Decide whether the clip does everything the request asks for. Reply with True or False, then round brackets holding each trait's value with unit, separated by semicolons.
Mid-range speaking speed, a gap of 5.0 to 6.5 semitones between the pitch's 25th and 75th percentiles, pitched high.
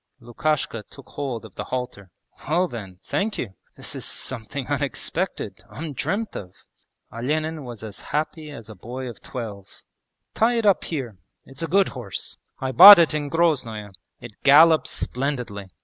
False (155 wpm; 5.6 semitones; 135 Hz)